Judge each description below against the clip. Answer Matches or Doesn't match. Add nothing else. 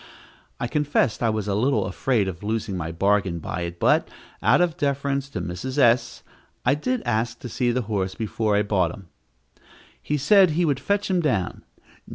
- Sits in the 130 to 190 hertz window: Doesn't match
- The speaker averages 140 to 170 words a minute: Doesn't match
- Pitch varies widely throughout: Matches